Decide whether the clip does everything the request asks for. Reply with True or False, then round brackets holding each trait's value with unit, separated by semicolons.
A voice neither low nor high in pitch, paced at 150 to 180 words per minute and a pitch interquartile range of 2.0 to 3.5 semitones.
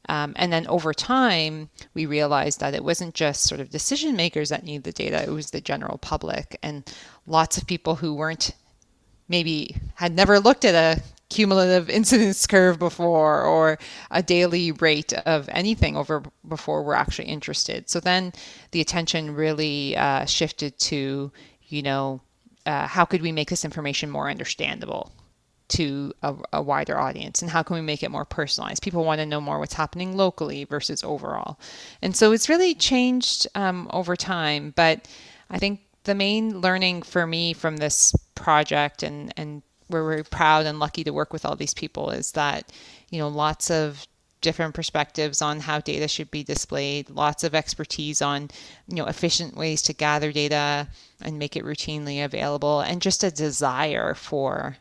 True (155 Hz; 175 wpm; 3.0 semitones)